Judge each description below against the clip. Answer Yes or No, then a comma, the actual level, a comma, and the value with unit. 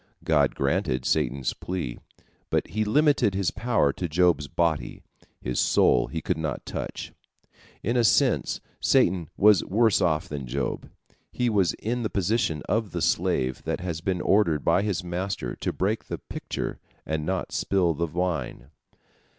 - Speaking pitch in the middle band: No, very low, 90 Hz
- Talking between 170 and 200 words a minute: No, average, 160 wpm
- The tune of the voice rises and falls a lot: No, average, 4.9 semitones